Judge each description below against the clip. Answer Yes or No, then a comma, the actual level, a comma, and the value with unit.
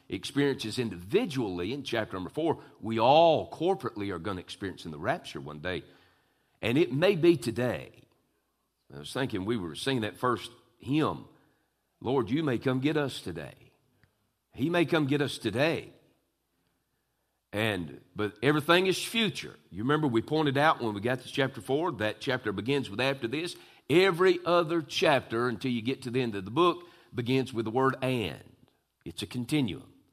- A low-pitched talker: Yes, low, 130 Hz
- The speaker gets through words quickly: No, average, 175 wpm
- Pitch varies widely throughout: Yes, wide, 5.7 semitones